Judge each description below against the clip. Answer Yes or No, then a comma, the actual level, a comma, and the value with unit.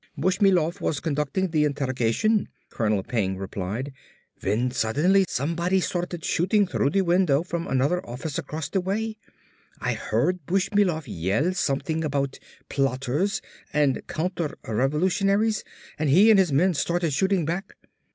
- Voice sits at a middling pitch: Yes, medium, 160 Hz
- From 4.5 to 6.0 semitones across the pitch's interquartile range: Yes, wide, 5.5 semitones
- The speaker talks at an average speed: No, slow, 130 wpm